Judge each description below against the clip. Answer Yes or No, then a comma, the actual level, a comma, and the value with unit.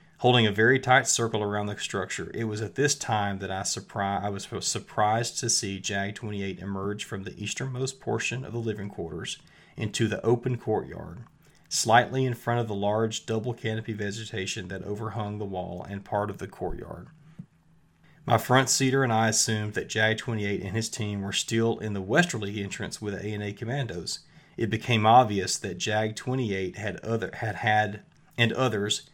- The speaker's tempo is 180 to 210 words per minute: Yes, average, 185 wpm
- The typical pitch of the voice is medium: No, low, 110 Hz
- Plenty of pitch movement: No, average, 2.7 semitones